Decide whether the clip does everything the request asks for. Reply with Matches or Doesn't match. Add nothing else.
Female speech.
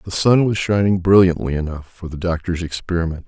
Doesn't match